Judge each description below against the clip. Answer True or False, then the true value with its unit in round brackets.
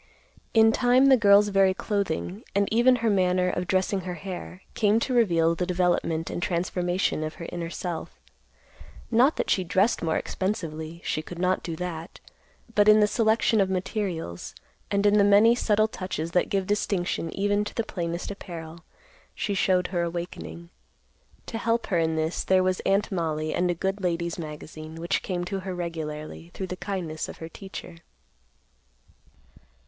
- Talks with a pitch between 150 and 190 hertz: True (185 Hz)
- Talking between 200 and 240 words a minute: False (170 wpm)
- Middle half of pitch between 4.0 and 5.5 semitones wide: False (3.2 semitones)